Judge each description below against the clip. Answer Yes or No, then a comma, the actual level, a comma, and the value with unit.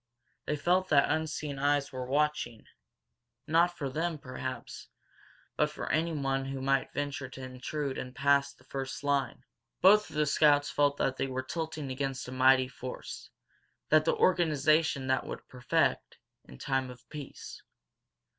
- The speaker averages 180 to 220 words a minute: No, average, 155 wpm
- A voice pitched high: No, medium, 140 Hz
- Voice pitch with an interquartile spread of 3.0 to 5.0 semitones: No, narrow, 2.6 semitones